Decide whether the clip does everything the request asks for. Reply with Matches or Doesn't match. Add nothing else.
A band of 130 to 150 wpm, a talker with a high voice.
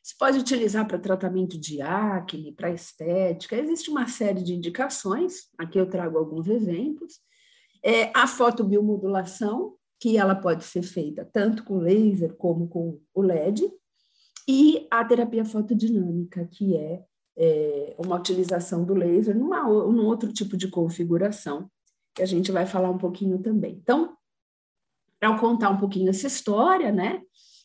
Matches